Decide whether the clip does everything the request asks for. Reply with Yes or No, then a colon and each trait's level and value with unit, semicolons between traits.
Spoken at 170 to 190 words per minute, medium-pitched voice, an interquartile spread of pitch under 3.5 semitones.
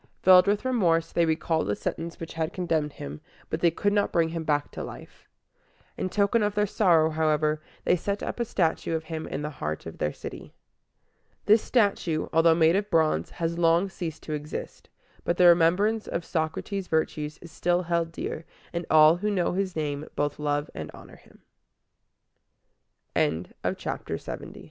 Yes: average, 185 wpm; medium, 165 Hz; average, 2.8 semitones